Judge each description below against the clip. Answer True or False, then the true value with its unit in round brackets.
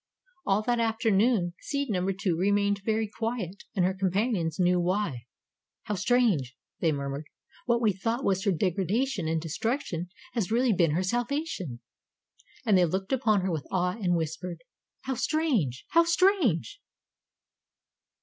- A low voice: False (195 Hz)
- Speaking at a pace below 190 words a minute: True (145 wpm)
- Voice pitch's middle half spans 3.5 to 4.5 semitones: False (5.1 semitones)